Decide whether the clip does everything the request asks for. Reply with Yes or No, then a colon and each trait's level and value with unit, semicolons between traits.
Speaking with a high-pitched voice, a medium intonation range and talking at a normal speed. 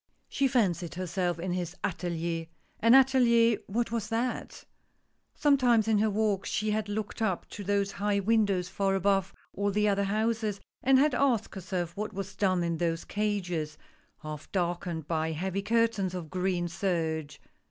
Yes: high, 195 Hz; average, 3.7 semitones; average, 160 wpm